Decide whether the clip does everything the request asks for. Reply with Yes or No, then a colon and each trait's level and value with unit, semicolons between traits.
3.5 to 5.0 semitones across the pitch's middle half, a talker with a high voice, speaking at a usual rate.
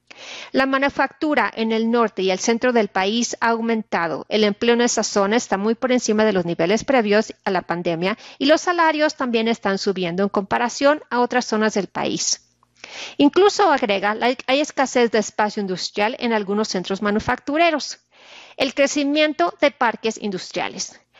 Yes: average, 4.7 semitones; high, 230 Hz; average, 165 wpm